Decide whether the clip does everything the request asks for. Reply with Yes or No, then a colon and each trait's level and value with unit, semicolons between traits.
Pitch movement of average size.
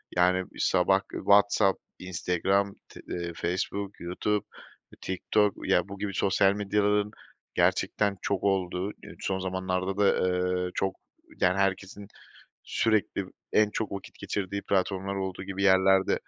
No: narrow, 1.4 semitones